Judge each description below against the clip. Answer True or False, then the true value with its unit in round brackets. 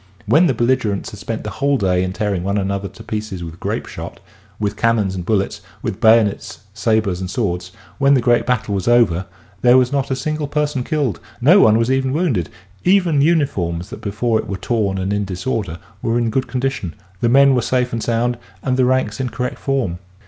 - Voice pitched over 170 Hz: False (115 Hz)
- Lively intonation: False (4.9 semitones)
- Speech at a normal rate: False (210 wpm)